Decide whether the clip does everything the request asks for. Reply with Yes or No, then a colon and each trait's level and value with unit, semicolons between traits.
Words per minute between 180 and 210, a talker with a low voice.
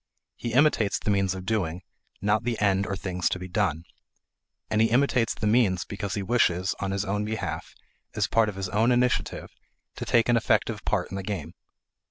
Yes: average, 200 wpm; low, 100 Hz